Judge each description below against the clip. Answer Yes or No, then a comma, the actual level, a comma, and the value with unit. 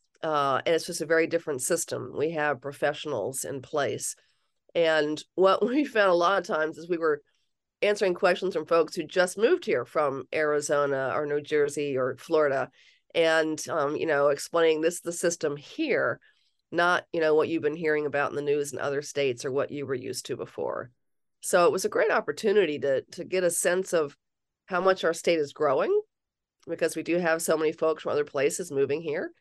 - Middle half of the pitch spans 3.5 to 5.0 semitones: Yes, average, 4.3 semitones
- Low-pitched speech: No, medium, 165 Hz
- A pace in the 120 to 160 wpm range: No, fast, 205 wpm